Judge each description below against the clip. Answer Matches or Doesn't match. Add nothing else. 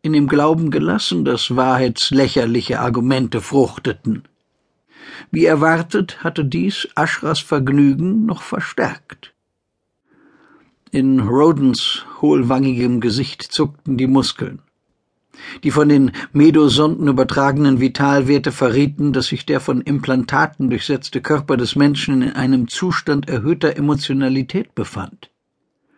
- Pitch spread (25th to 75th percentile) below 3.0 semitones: Matches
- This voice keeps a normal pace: Doesn't match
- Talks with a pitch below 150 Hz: Matches